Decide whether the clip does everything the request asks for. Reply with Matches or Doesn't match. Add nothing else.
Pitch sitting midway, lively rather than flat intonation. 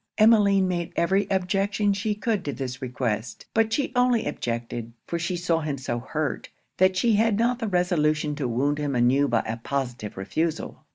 Matches